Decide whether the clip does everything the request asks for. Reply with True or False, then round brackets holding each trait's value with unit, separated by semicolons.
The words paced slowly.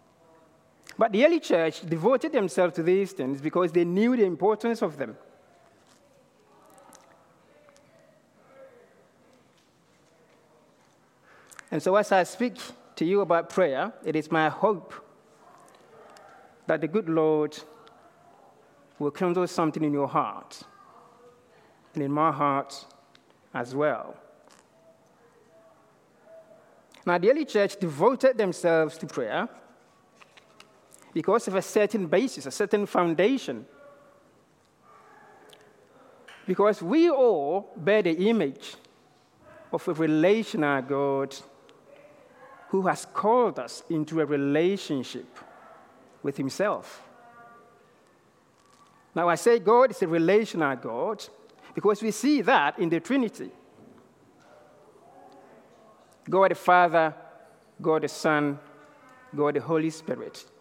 True (105 wpm)